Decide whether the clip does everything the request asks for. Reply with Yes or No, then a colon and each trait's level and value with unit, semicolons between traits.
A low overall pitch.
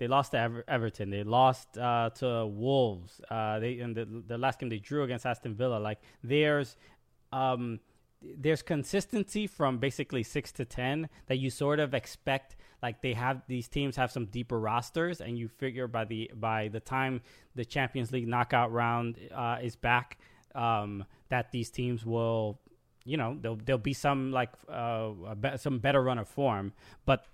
Yes: low, 125 Hz